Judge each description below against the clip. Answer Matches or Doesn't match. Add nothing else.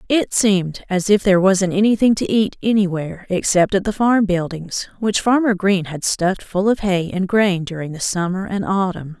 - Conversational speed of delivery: Matches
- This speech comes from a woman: Matches